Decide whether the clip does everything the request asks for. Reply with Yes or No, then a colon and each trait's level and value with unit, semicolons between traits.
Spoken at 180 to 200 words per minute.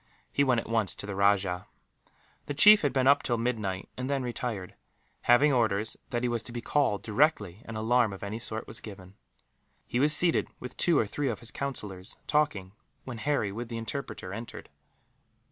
Yes: average, 195 wpm